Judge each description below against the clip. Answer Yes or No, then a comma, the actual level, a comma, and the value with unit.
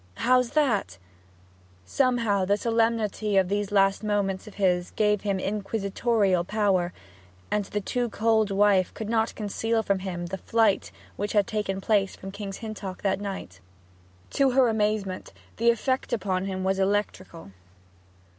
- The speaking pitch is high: Yes, high, 205 Hz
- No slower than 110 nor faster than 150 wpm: Yes, average, 145 wpm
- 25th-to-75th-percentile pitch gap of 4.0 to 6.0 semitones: No, narrow, 2.4 semitones